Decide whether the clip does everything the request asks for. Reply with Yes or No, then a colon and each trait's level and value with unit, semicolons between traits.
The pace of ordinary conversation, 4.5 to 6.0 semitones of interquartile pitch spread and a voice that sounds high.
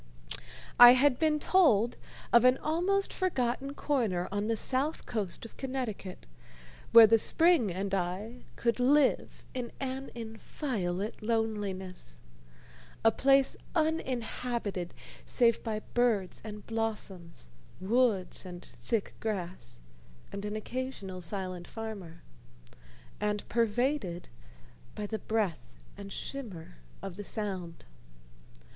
No: slow, 110 wpm; average, 4.8 semitones; high, 220 Hz